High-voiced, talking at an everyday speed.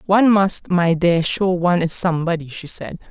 No: medium, 175 Hz; average, 195 wpm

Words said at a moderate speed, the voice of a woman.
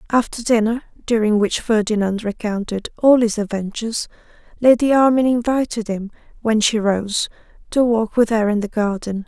Yes: average, 150 wpm; female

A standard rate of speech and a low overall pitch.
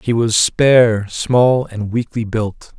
Yes: average, 150 wpm; low, 115 Hz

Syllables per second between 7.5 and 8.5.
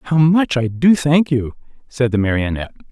No: 5.0 syllables/s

